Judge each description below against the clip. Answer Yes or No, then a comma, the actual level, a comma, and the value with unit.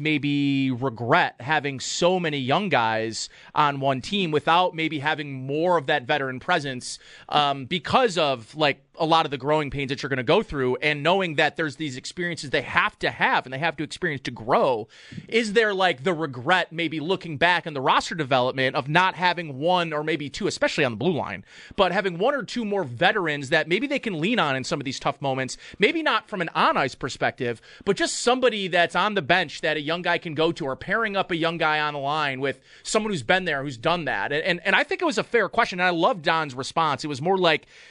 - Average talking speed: No, fast, 235 wpm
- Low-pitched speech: No, medium, 160 Hz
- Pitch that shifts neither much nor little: Yes, average, 4.3 semitones